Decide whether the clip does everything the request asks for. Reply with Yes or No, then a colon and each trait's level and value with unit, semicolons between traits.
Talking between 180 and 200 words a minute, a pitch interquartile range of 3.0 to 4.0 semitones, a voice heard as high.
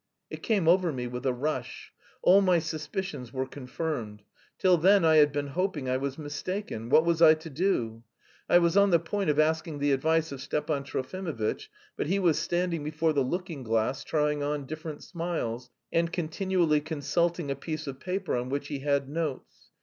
No: average, 190 wpm; average, 3.7 semitones; medium, 155 Hz